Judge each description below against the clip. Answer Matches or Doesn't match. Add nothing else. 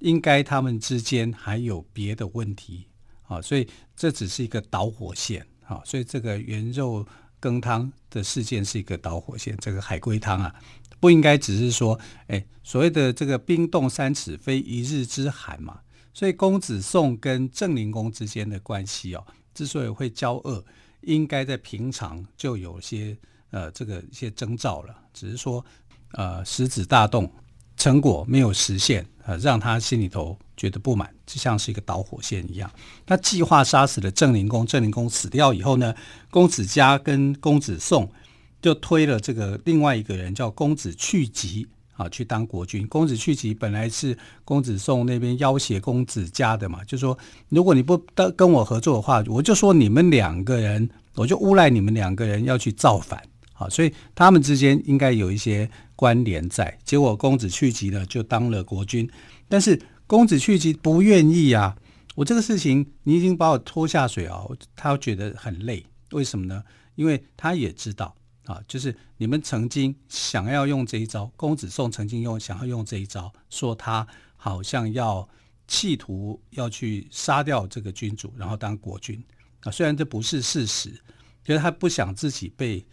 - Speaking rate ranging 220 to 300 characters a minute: Matches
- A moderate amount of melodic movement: Matches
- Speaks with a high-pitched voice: Doesn't match